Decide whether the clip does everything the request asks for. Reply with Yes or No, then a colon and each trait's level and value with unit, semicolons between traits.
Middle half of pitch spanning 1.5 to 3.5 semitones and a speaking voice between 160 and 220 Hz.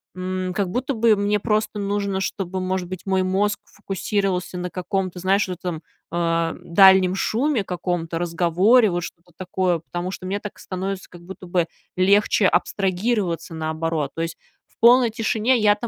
Yes: average, 2.7 semitones; medium, 185 Hz